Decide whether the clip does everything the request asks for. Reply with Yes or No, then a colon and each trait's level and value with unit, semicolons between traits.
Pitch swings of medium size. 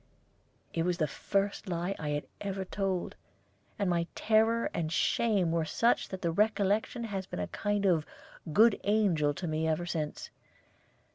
Yes: average, 4.0 semitones